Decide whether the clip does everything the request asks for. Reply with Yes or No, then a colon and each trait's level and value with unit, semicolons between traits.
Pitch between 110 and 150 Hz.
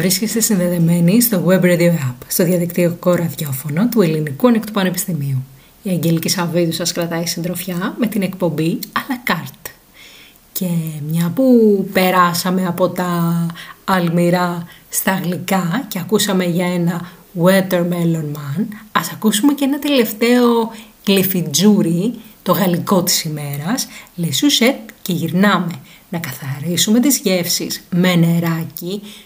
No: medium, 180 Hz